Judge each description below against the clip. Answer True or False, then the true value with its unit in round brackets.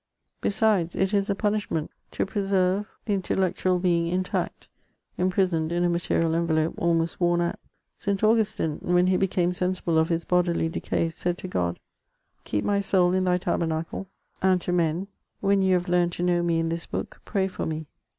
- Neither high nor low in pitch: True (180 Hz)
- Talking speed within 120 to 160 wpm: False (180 wpm)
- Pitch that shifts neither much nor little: False (2.2 semitones)